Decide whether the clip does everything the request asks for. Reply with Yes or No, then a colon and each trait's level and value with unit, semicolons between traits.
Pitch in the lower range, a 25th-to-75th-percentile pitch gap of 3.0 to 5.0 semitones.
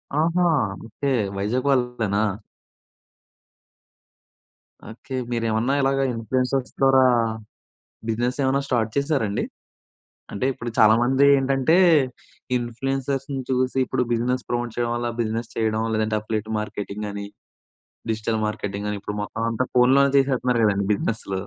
Yes: low, 120 Hz; average, 3.3 semitones